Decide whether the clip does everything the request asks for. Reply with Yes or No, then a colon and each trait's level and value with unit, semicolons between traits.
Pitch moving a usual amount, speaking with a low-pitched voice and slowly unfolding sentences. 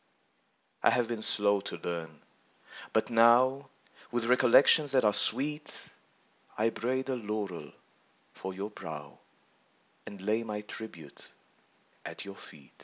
Yes: average, 4.0 semitones; low, 110 Hz; slow, 130 wpm